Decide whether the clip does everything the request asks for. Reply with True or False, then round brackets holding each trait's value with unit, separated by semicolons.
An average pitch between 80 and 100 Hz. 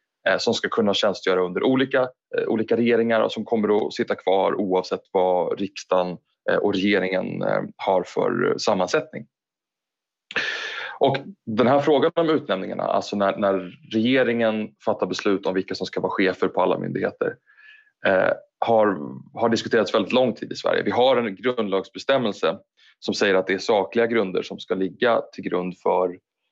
False (110 Hz)